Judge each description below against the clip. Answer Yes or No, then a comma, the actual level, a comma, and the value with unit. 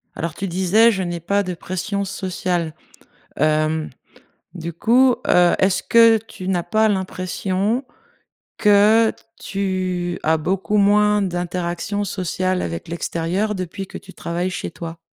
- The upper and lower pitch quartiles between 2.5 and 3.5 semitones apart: Yes, average, 2.9 semitones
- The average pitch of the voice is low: No, medium, 185 Hz